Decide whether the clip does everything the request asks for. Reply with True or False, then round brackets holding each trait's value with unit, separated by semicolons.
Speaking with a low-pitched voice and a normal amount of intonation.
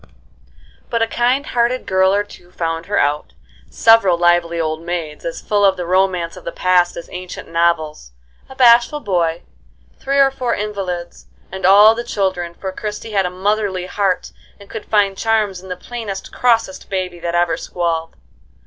False (190 Hz; 3.7 semitones)